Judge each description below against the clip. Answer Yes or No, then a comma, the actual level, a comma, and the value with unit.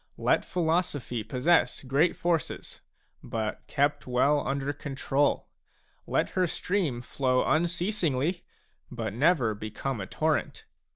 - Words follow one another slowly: Yes, slow, 115 wpm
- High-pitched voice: No, medium, 140 Hz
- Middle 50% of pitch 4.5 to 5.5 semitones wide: Yes, average, 5.0 semitones